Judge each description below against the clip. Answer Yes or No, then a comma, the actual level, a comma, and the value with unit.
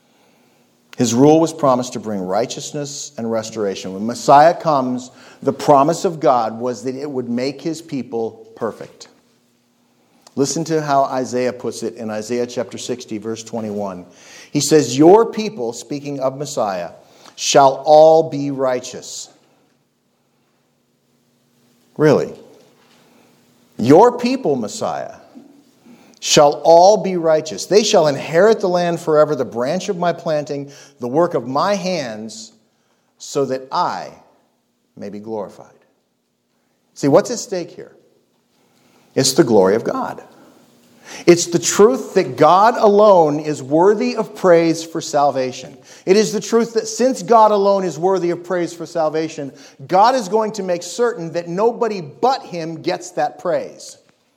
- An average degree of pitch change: No, wide, 6.5 semitones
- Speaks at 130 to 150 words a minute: Yes, average, 140 wpm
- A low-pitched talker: No, medium, 150 Hz